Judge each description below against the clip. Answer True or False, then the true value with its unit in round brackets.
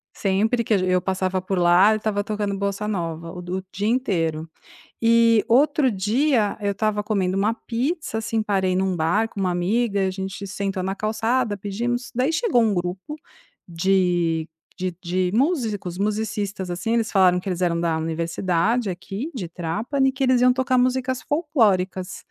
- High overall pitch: True (200 Hz)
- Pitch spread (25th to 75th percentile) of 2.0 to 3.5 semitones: False (4.1 semitones)